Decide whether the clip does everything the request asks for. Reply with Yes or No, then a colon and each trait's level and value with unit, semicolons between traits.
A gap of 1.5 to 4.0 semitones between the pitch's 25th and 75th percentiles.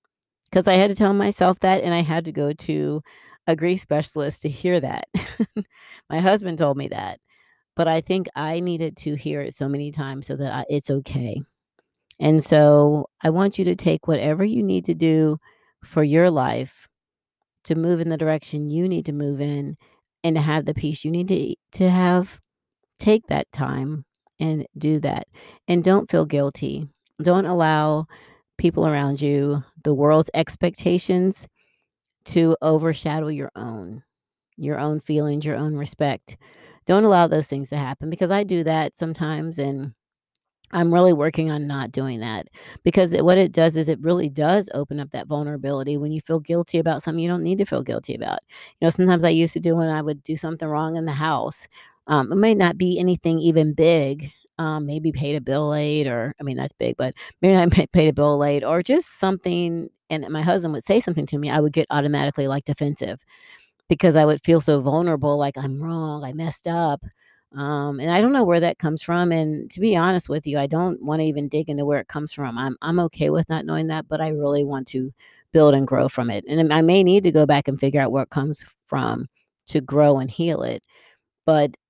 Yes: average, 2.9 semitones